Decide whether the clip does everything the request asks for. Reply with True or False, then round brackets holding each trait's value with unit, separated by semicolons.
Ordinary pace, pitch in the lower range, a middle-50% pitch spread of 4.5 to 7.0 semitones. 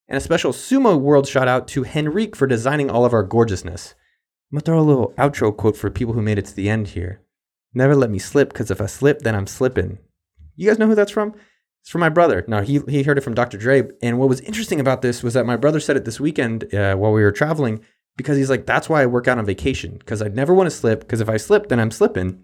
False (275 wpm; 125 Hz; 5.1 semitones)